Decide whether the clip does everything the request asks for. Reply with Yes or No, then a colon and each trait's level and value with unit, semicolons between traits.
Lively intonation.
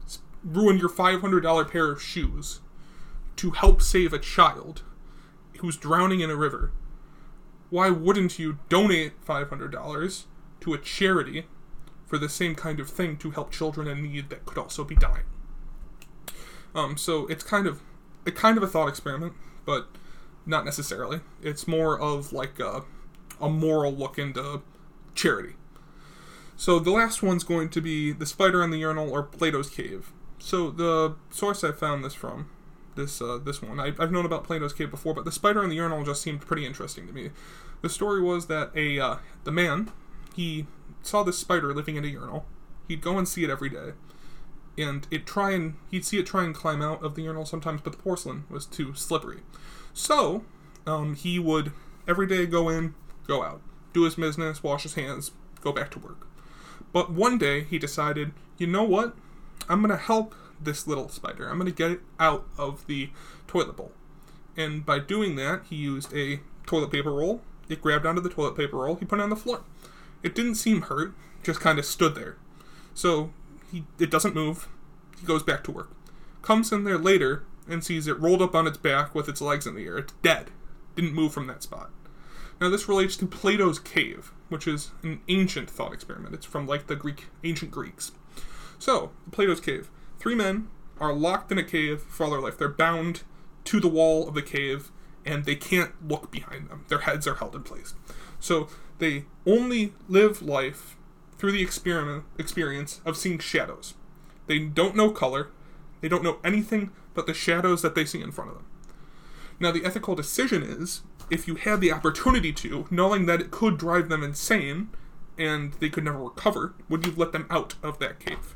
No: average, 2.8 semitones